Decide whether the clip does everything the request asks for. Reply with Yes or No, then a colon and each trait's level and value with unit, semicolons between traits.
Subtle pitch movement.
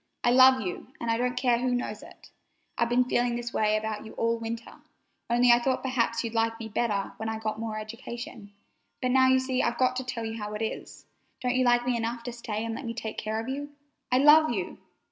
Yes: narrow, 2.1 semitones